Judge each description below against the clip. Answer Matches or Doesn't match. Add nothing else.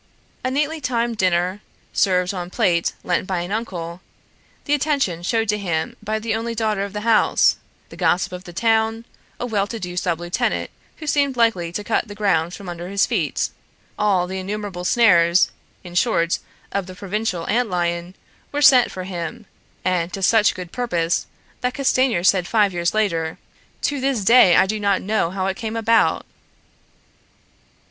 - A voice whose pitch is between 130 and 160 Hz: Doesn't match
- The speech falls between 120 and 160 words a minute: Doesn't match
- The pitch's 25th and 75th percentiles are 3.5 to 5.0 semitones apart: Matches